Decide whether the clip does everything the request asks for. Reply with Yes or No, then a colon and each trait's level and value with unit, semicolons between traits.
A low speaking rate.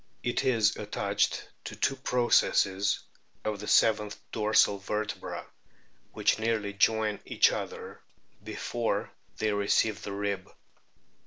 Yes: slow, 110 wpm